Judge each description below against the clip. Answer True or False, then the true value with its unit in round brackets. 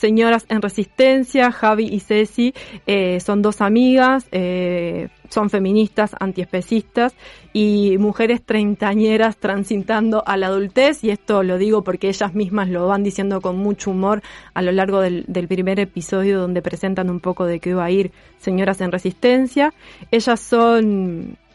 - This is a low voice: False (205 Hz)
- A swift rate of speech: False (155 wpm)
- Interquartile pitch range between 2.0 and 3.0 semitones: True (2.6 semitones)